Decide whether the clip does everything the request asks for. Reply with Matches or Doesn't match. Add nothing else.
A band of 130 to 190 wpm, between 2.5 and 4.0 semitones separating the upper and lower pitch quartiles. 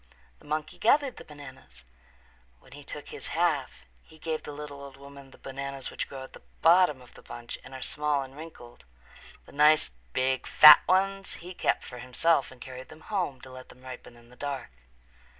Doesn't match